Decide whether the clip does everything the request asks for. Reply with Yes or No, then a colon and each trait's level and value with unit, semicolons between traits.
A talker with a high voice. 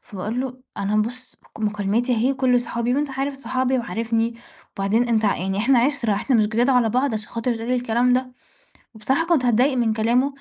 Yes: high, 240 Hz